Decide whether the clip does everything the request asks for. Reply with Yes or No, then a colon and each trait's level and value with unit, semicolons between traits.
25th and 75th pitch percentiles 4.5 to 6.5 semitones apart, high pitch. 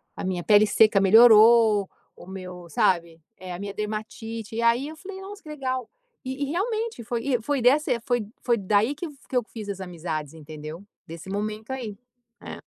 Yes: average, 5.2 semitones; high, 220 Hz